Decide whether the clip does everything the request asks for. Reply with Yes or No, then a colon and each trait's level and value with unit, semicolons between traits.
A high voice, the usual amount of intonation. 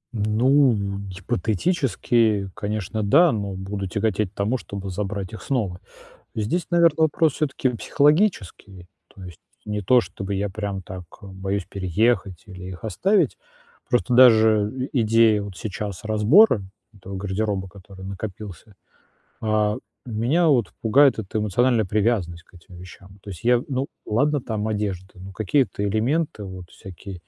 No: low, 105 Hz; average, 3.9 semitones